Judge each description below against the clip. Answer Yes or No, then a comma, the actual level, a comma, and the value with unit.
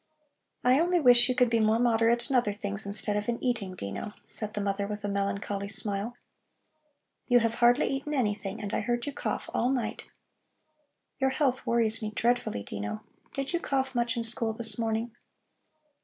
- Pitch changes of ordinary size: Yes, average, 3.1 semitones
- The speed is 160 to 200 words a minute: Yes, average, 185 wpm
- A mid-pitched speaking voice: No, high, 230 Hz